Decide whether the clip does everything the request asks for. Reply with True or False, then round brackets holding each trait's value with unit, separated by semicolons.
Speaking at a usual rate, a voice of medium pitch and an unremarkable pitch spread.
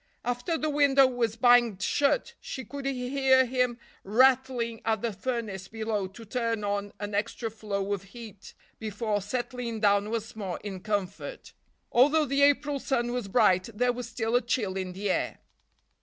False (165 wpm; 230 Hz; 3.8 semitones)